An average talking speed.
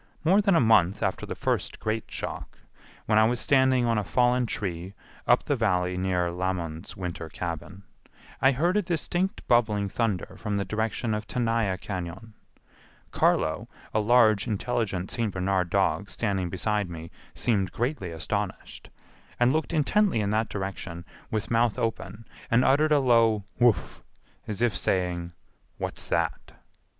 Yes: average, 150 wpm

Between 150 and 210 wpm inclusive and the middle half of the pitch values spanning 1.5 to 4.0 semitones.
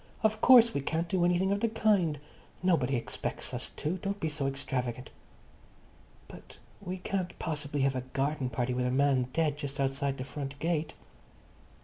No: average, 170 wpm; average, 4.9 semitones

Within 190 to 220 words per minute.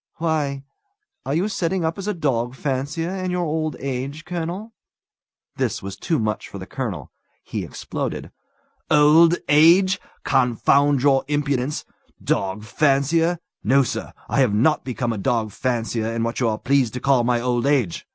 No: average, 160 wpm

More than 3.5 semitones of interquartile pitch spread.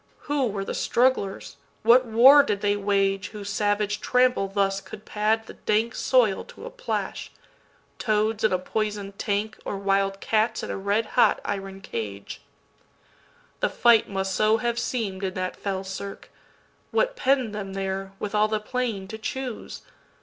No: average, 2.7 semitones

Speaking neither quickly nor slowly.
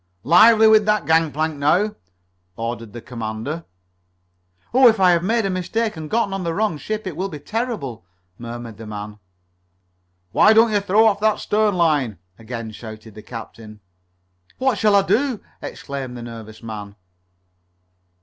Yes: average, 160 wpm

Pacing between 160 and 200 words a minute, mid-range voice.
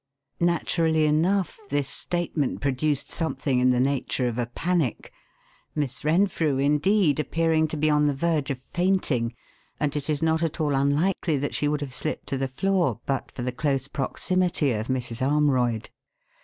Yes: average, 170 wpm; medium, 145 Hz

